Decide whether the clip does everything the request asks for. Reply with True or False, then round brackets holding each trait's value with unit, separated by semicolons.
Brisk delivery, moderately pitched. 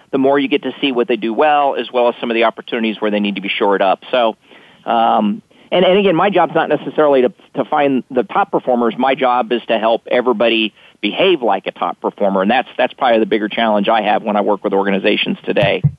False (245 wpm; 125 Hz)